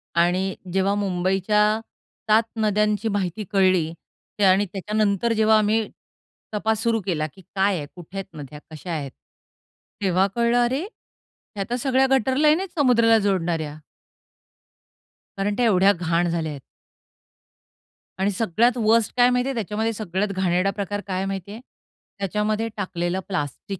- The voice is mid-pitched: No, high, 200 Hz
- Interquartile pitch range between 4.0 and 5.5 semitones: No, average, 3.3 semitones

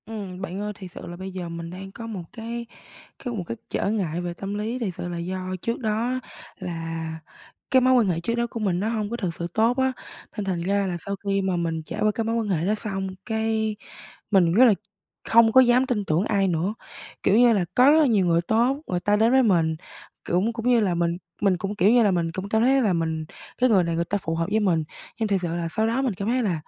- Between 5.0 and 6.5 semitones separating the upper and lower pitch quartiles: No, average, 4.5 semitones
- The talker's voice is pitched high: Yes, high, 200 Hz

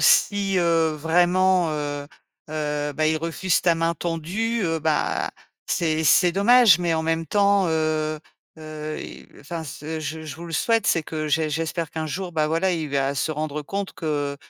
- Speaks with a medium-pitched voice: Yes, medium, 160 Hz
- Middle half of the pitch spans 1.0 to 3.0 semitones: Yes, narrow, 2.4 semitones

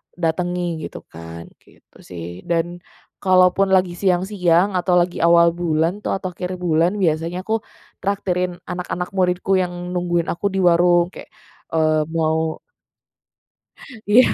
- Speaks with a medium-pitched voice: Yes, medium, 175 Hz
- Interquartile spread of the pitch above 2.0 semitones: No, narrow, 1.6 semitones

